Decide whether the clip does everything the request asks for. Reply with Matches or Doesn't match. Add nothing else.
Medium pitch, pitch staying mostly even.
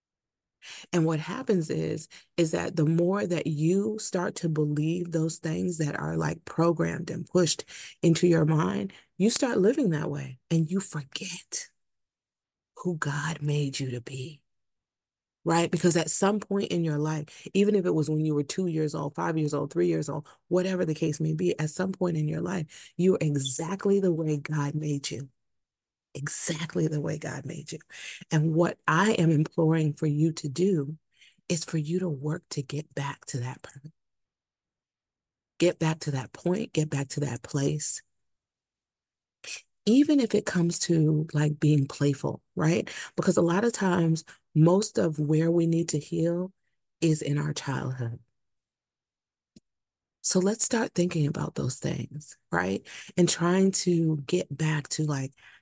Doesn't match